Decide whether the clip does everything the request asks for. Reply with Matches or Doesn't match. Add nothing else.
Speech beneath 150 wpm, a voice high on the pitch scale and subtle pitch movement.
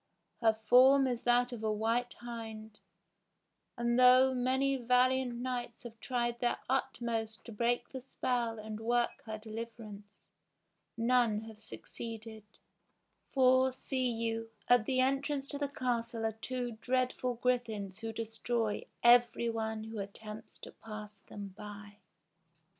Matches